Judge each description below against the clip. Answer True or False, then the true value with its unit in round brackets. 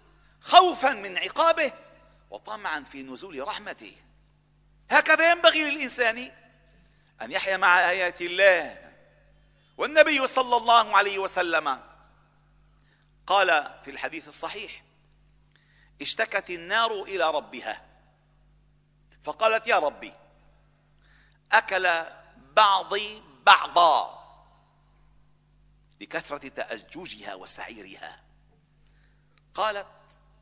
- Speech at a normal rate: True (75 wpm)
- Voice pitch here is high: False (180 Hz)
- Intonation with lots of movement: True (7.1 semitones)